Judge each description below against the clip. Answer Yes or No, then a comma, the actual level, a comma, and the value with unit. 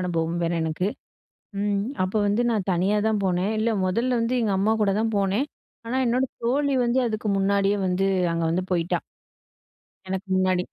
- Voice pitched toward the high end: Yes, high, 200 Hz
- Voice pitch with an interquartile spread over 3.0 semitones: Yes, average, 3.6 semitones